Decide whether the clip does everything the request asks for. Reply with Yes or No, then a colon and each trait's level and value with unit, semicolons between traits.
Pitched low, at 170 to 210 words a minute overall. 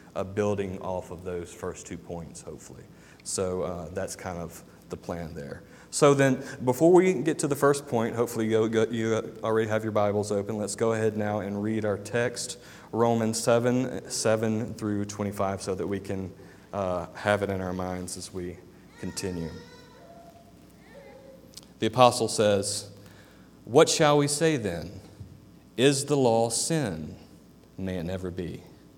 No: low, 105 Hz; average, 160 wpm